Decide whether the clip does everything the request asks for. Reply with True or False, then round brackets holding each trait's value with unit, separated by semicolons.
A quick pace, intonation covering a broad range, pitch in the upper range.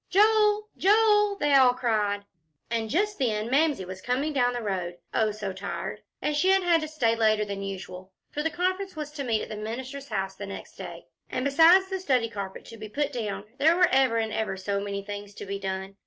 True (220 wpm; 7.4 semitones; 240 Hz)